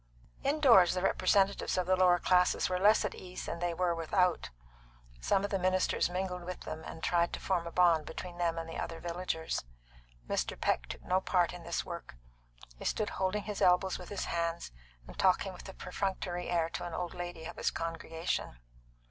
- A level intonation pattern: Yes, narrow, 1.8 semitones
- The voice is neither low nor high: Yes, medium, 180 Hz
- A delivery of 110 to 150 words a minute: No, average, 200 wpm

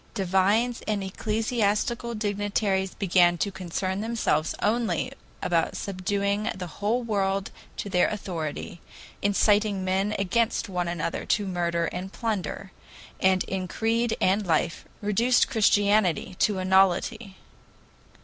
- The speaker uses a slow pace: Yes, slow, 120 wpm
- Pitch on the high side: Yes, high, 200 Hz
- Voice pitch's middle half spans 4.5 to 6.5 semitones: No, narrow, 2.5 semitones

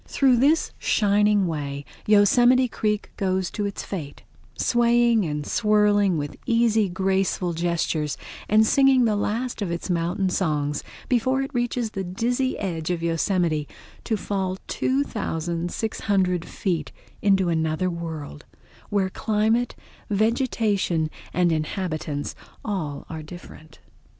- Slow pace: Yes, slow, 115 wpm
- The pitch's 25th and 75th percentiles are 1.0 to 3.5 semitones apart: No, average, 4.9 semitones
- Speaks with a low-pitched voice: No, high, 195 Hz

